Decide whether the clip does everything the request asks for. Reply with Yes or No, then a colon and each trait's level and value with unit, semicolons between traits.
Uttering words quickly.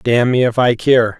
Yes: fast, 250 wpm